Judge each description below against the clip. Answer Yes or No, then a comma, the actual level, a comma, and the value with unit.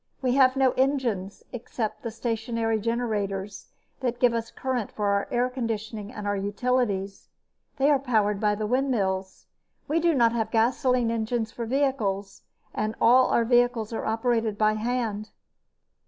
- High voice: Yes, high, 230 Hz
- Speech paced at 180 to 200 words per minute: No, average, 150 wpm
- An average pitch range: Yes, average, 3.0 semitones